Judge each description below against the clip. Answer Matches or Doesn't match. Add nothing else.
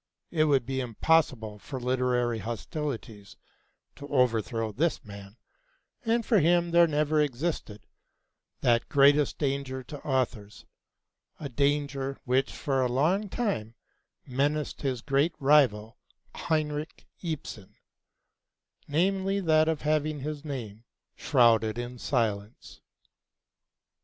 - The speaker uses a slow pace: Matches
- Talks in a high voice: Doesn't match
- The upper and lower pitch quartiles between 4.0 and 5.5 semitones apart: Matches